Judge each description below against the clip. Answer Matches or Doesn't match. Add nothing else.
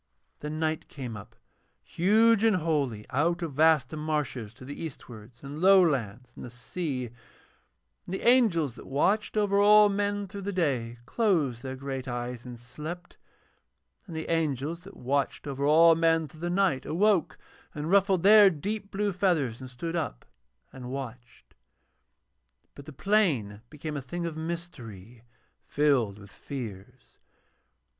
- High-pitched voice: Doesn't match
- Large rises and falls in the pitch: Matches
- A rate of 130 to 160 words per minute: Matches